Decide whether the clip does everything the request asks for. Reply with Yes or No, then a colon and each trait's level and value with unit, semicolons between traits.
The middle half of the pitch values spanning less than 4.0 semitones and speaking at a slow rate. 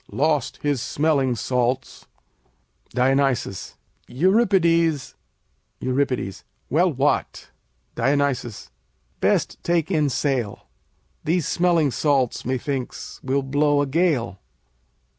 Yes: average, 3.6 semitones; slow, 85 wpm